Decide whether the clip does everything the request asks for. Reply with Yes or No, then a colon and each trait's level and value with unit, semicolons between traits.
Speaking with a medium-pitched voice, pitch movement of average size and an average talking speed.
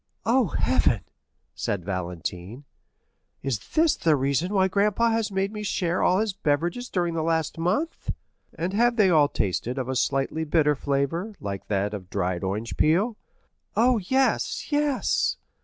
No: medium, 165 Hz; wide, 8.3 semitones; average, 155 wpm